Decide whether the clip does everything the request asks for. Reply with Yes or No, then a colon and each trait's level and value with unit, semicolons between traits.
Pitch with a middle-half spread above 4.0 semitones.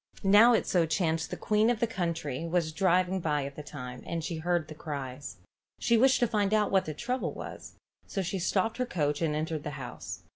Yes: average, 5.1 semitones